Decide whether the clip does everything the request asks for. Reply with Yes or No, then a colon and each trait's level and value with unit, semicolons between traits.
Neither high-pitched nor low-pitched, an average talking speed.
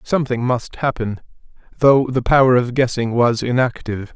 No: low, 125 Hz; average, 145 wpm